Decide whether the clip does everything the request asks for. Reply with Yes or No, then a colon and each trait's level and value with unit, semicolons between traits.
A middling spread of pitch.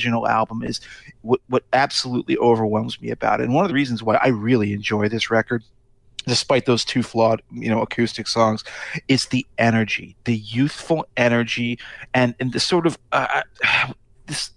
No: narrow, 2.2 semitones